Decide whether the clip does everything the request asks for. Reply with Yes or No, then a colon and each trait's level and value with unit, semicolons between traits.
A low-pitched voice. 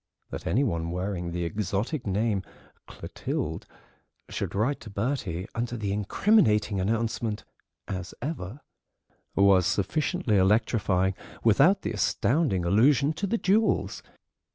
Yes: low, 105 Hz